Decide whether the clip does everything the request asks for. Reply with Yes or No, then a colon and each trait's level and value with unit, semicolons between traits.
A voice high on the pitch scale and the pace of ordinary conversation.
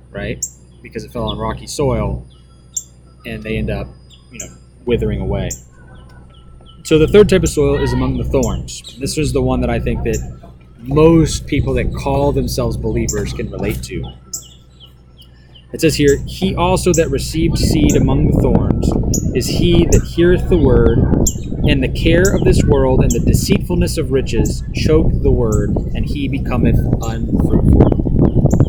No: low, 105 Hz; average, 160 wpm